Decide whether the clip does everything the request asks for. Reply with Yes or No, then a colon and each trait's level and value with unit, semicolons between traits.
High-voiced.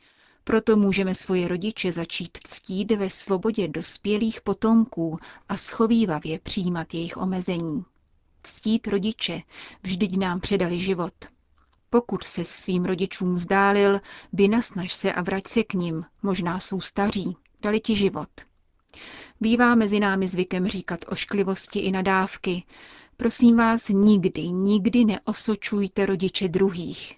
Yes: high, 195 Hz